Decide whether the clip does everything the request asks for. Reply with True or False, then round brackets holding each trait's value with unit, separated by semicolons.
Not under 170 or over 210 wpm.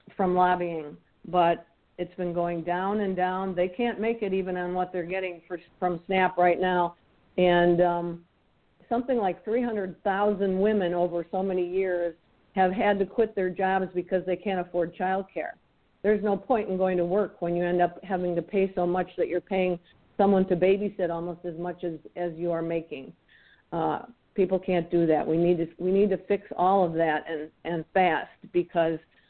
True (190 wpm)